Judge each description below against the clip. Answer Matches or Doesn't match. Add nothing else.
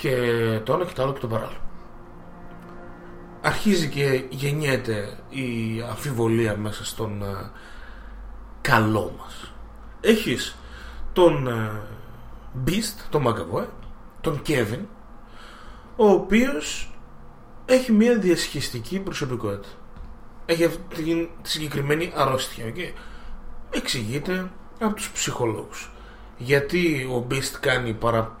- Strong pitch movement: Matches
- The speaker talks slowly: Matches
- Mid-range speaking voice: Doesn't match